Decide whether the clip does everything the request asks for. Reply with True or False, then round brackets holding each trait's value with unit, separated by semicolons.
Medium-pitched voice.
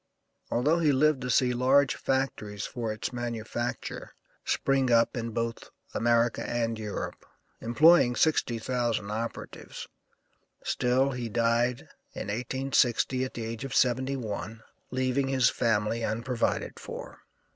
False (120 Hz)